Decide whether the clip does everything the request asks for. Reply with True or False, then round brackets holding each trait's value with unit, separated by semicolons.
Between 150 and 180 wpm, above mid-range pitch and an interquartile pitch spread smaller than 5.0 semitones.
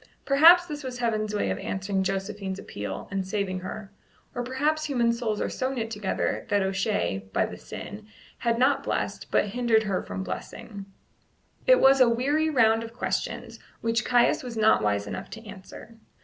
True (175 wpm; 225 Hz; 4.2 semitones)